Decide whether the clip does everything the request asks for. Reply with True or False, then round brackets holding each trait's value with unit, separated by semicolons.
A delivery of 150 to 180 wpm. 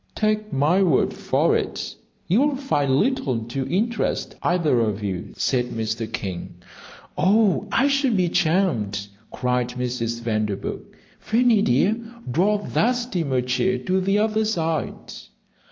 False (135 wpm)